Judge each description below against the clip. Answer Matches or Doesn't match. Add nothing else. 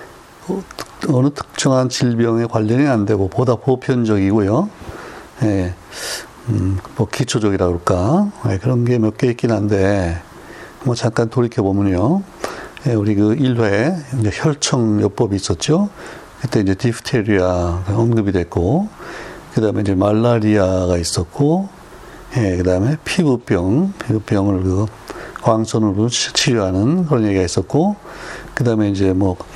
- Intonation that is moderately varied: Matches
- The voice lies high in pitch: Doesn't match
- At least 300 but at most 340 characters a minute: Doesn't match